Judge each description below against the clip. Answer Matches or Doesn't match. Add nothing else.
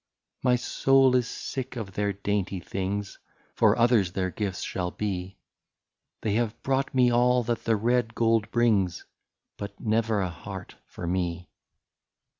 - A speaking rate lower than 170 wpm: Matches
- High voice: Doesn't match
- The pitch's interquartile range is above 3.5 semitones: Matches